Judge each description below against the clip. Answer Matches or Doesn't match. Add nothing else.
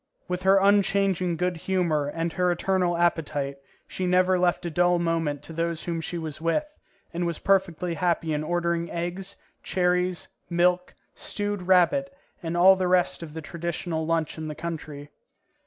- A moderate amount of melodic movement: Doesn't match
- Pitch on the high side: Doesn't match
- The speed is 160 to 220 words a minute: Matches